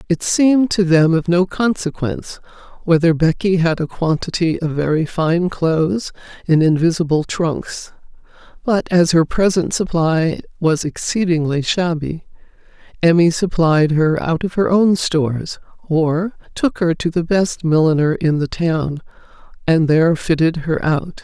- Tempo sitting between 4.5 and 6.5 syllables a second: No, 4.3 syllables/s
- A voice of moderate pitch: Yes, medium, 165 Hz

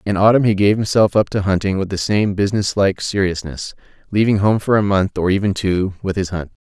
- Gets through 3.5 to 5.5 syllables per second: No, 5.7 syllables/s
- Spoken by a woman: No, male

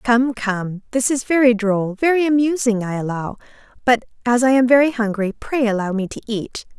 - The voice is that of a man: No, female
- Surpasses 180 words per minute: No, average, 170 wpm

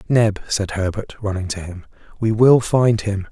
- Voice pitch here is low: Yes, low, 105 Hz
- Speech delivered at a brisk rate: No, average, 180 wpm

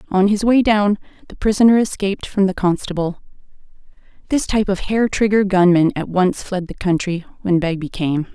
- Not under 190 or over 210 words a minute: No, average, 175 wpm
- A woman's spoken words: Yes, female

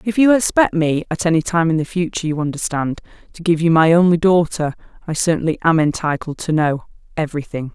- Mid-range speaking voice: Yes, medium, 165 Hz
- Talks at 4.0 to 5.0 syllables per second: No, 6.1 syllables/s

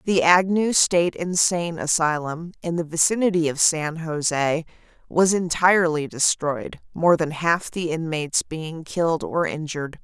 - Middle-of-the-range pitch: Yes, medium, 165 Hz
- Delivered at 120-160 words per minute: Yes, average, 140 wpm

